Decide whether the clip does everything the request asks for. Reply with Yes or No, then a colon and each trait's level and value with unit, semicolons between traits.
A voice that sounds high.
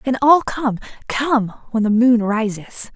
Yes: high, 235 Hz